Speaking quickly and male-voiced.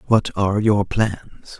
No: average, 150 wpm; male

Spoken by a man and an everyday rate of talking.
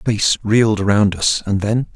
Yes: male; average, 185 wpm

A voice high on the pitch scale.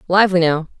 No: medium, 175 Hz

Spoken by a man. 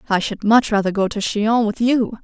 No: female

